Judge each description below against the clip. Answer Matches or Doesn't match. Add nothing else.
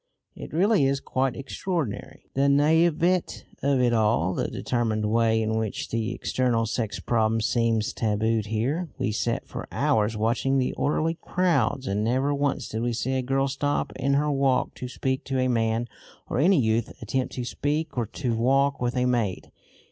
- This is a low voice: Matches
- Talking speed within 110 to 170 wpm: Doesn't match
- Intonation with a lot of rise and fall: Doesn't match